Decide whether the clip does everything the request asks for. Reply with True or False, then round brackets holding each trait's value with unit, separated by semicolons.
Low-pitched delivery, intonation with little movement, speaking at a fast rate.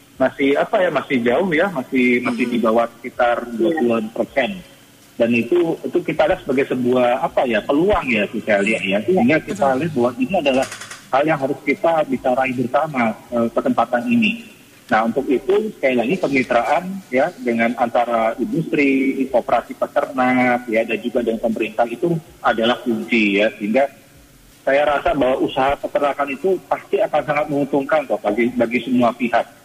False (130 Hz; 3.5 semitones; 160 wpm)